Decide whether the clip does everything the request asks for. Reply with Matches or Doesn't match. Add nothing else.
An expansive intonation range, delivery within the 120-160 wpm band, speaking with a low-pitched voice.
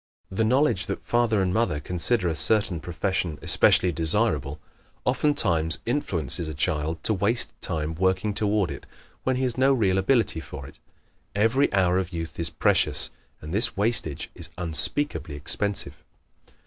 Matches